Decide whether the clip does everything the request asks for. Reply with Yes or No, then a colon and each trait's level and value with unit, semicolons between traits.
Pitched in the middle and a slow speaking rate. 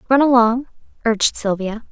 No: high, 235 Hz; slow, 125 wpm